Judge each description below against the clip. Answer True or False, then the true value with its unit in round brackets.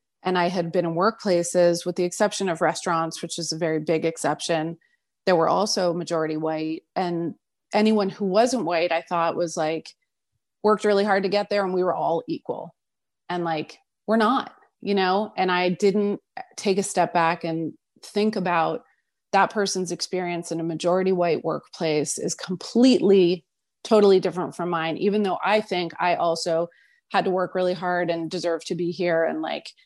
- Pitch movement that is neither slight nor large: True (3.1 semitones)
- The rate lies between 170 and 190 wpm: True (180 wpm)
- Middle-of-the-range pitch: True (180 Hz)